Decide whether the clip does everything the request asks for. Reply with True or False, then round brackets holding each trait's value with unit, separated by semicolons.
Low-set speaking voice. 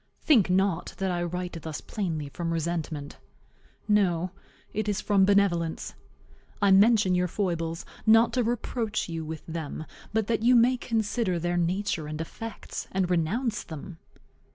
False (185 Hz)